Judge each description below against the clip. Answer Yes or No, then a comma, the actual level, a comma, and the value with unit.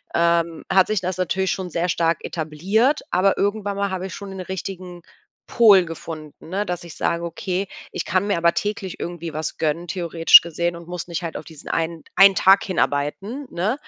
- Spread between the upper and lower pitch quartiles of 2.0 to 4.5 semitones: Yes, narrow, 2.5 semitones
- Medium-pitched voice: Yes, medium, 180 Hz